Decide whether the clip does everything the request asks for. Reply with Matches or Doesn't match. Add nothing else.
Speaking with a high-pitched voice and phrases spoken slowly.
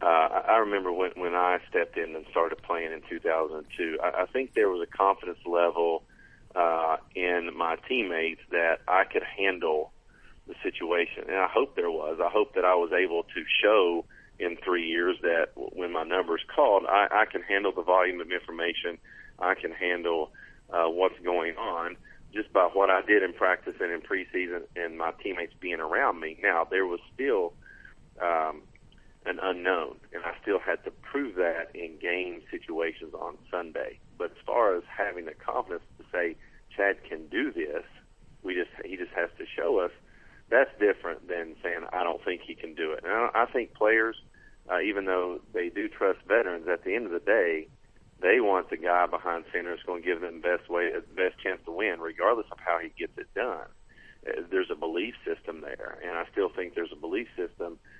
Doesn't match